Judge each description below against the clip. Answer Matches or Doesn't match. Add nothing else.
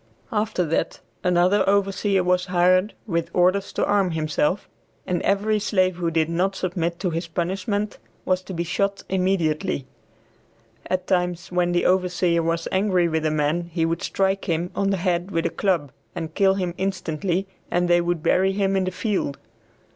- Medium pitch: Matches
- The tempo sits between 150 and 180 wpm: Matches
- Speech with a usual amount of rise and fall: Doesn't match